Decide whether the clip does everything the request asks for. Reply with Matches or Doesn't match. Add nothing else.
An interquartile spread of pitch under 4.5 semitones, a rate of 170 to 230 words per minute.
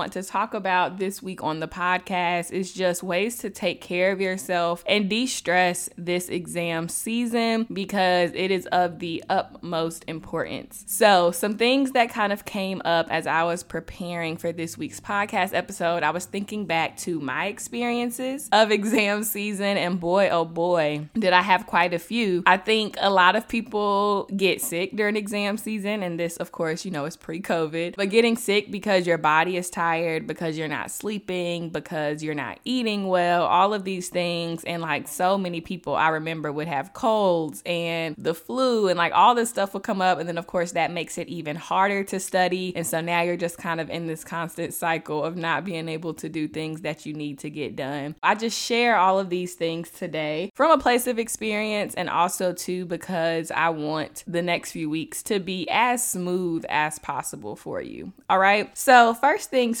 Matches